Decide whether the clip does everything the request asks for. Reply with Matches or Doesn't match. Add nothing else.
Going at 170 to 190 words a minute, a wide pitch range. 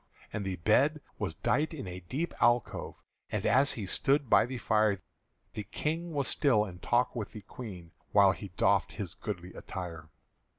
Matches